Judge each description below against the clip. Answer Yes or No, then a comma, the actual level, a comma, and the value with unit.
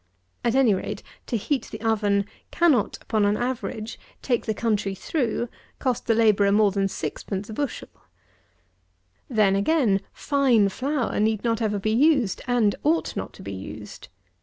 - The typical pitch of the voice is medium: No, high, 220 Hz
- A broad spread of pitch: No, average, 3.8 semitones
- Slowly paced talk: No, average, 160 wpm